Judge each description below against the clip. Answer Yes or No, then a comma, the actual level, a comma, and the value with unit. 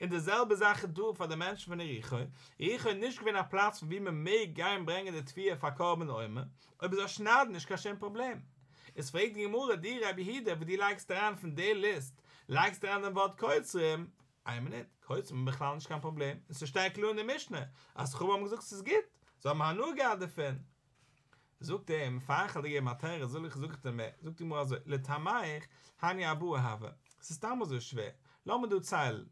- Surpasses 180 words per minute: Yes, average, 200 wpm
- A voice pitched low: No, medium, 165 Hz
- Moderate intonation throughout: No, wide, 6.2 semitones